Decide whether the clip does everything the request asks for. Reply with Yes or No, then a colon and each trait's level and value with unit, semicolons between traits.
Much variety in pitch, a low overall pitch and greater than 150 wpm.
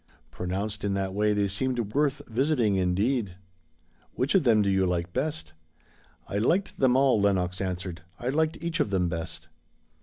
Yes: wide, 6.0 semitones; low, 105 Hz; average, 175 wpm